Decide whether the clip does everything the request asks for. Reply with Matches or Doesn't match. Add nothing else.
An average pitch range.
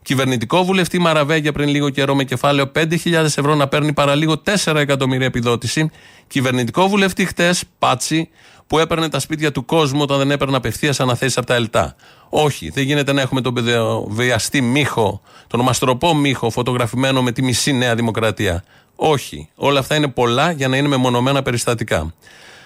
Matches